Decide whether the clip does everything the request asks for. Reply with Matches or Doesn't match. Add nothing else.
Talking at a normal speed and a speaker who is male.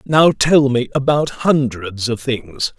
Matches